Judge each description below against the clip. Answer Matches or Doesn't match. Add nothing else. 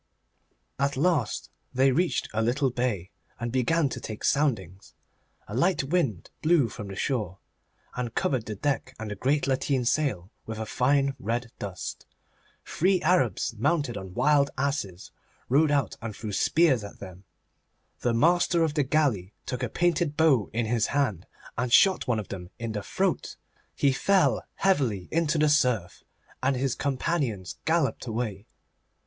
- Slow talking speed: Doesn't match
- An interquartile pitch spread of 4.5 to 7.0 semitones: Matches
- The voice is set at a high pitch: Doesn't match